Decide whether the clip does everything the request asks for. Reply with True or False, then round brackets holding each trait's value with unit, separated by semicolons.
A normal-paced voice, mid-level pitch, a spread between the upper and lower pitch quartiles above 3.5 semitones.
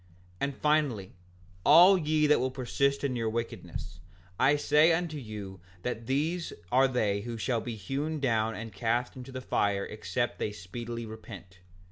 False (165 wpm; 120 Hz; 4.7 semitones)